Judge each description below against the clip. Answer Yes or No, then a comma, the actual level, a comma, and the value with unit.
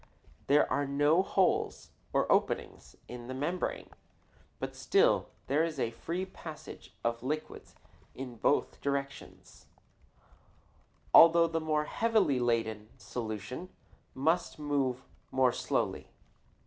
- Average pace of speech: No, slow, 110 wpm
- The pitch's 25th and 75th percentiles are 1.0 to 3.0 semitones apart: No, average, 4.6 semitones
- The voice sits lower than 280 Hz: Yes, medium, 140 Hz